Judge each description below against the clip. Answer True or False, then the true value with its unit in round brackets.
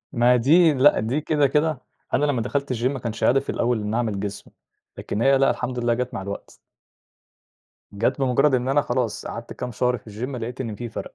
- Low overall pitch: True (125 Hz)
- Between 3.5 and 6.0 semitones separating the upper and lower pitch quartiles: False (2.8 semitones)